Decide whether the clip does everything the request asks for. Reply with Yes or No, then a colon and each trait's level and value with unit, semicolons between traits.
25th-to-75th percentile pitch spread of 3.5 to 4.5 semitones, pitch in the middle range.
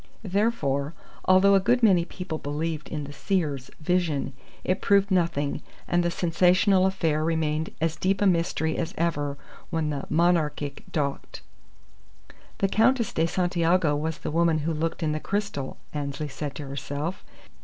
Yes: average, 3.8 semitones; medium, 165 Hz